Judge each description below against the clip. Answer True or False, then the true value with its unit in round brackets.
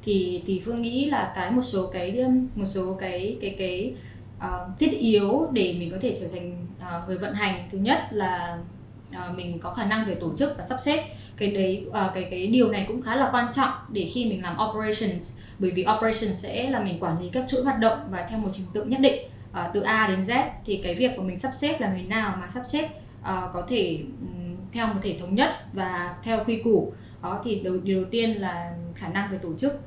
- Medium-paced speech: True (235 wpm)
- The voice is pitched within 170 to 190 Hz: False (205 Hz)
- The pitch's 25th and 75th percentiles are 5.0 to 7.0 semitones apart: False (4.2 semitones)